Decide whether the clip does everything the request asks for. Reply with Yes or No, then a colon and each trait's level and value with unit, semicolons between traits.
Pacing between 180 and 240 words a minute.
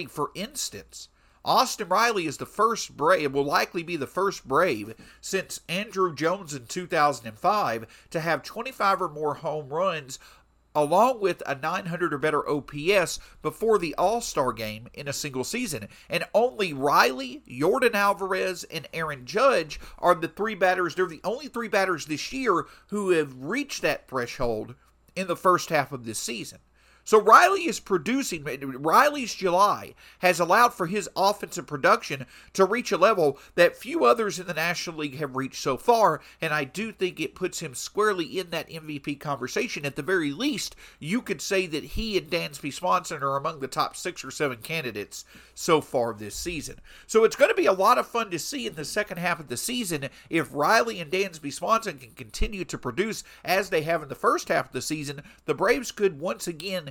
Yes: average, 190 wpm